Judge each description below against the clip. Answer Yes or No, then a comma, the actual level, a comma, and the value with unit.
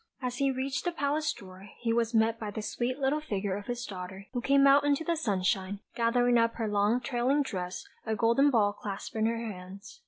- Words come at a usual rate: No, fast, 215 wpm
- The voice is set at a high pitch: Yes, high, 230 Hz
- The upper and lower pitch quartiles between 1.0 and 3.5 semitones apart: No, average, 4.6 semitones